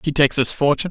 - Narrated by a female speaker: No, male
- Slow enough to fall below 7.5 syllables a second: No, 8.1 syllables/s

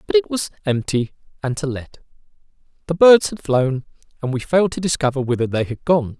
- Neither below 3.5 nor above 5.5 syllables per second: No, 5.7 syllables/s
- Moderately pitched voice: Yes, medium, 150 Hz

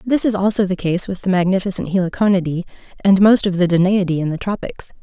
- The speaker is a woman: Yes, female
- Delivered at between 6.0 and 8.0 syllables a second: Yes, 6.3 syllables/s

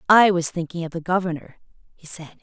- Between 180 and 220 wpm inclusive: Yes, average, 200 wpm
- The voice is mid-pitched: Yes, medium, 170 Hz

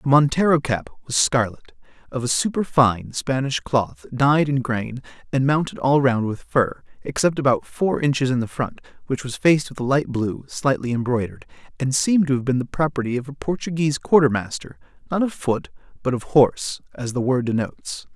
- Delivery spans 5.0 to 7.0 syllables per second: Yes, 5.4 syllables/s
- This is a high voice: No, low, 135 Hz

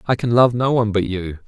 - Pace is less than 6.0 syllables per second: No, 6.2 syllables/s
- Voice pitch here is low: Yes, low, 110 Hz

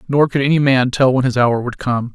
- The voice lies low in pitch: Yes, low, 130 Hz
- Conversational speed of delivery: No, fast, 280 wpm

